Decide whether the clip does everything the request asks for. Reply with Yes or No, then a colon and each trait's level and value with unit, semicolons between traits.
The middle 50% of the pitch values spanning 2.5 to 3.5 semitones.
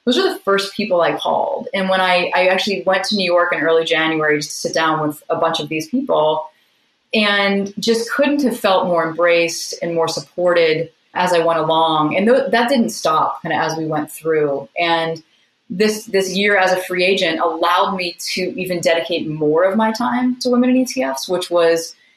No: average, 3.9 semitones